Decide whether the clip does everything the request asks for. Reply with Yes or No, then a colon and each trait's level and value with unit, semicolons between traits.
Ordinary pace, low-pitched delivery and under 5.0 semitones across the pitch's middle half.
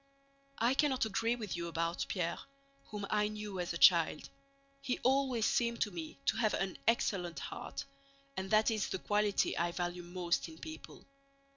No: average, 170 wpm; high, 200 Hz; average, 4.6 semitones